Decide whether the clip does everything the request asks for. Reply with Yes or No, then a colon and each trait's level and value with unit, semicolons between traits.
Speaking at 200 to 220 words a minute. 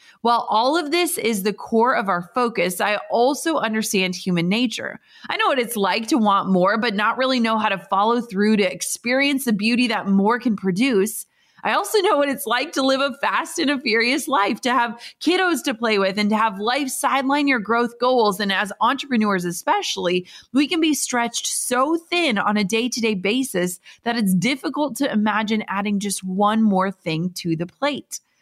Yes: fast, 205 wpm